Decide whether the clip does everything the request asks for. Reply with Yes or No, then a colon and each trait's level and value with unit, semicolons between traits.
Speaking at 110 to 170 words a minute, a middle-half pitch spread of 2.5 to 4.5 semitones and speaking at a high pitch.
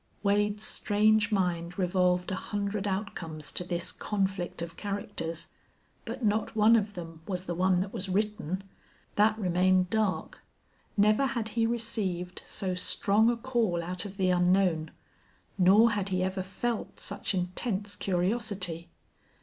Yes: average, 140 wpm; average, 2.8 semitones; high, 195 Hz